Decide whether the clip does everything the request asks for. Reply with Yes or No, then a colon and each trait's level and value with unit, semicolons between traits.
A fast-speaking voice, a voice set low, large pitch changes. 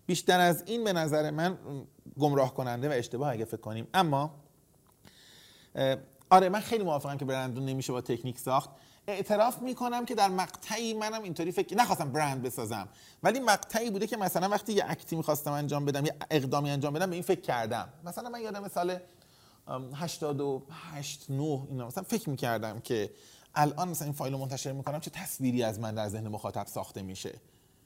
No: fast, 175 wpm; medium, 150 Hz; wide, 5.7 semitones